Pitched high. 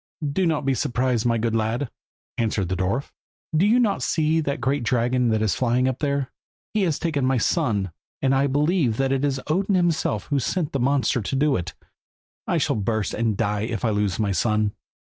No: low, 130 Hz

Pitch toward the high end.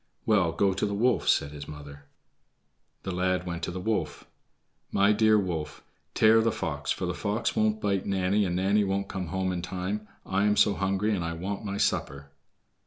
No: very low, 95 Hz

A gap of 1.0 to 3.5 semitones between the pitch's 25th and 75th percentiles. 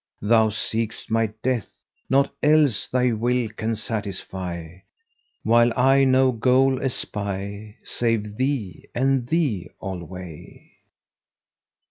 No: average, 4.1 semitones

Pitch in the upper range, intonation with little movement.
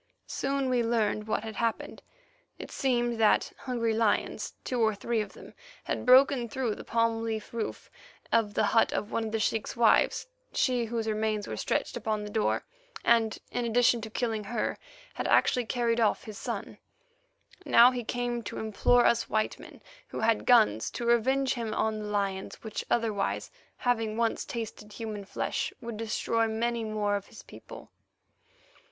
Yes: high, 225 Hz; narrow, 1.8 semitones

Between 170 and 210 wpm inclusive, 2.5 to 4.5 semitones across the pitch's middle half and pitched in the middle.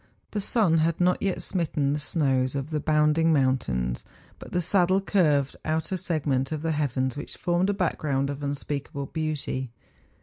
Yes: average, 175 wpm; average, 3.5 semitones; medium, 150 Hz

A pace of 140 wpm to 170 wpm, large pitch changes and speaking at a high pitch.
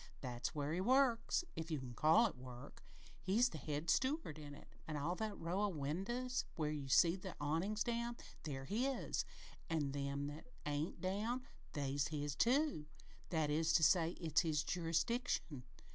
No: average, 165 wpm; wide, 6.5 semitones; medium, 160 Hz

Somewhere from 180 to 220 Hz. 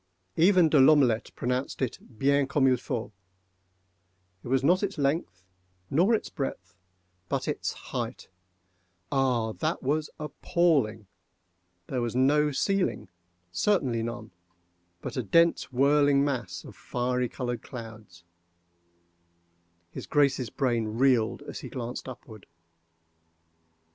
No: low, 125 Hz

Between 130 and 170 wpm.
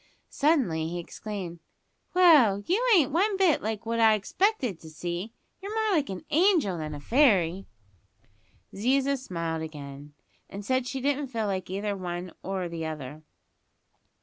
Yes: average, 155 wpm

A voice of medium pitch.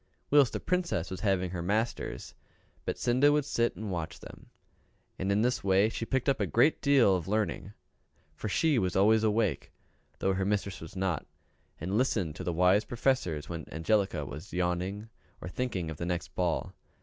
No: low, 100 Hz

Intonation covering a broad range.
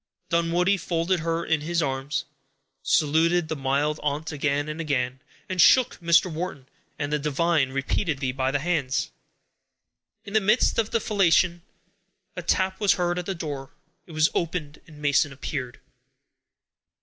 No: average, 3.6 semitones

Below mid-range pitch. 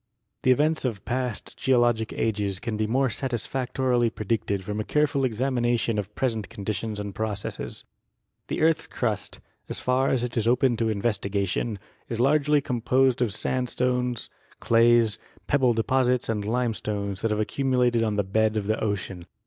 Yes: low, 115 Hz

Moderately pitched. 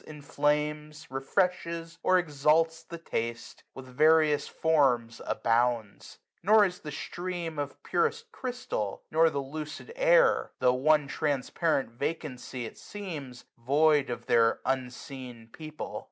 Yes: medium, 150 Hz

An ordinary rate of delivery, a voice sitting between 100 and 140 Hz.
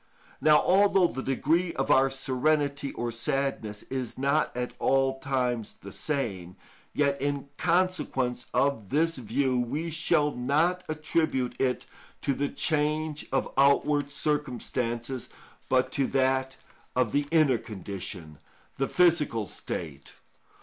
No: slow, 125 wpm; low, 135 Hz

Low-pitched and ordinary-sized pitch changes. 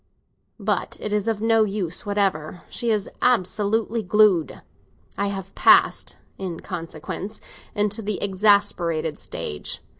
No: high, 200 Hz; average, 3.0 semitones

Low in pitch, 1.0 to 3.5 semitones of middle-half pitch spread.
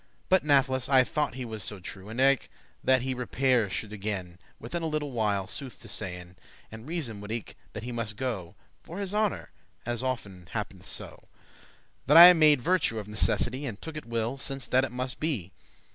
No: low, 125 Hz; average, 4.6 semitones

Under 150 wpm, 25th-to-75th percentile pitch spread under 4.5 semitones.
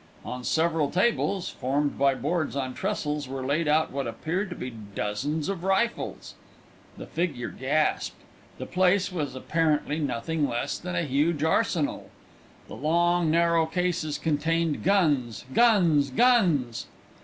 Yes: slow, 135 wpm; average, 3.9 semitones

